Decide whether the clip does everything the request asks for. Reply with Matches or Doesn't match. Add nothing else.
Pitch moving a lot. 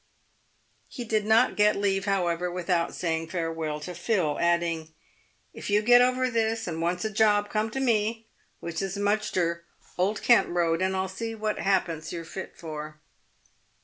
Doesn't match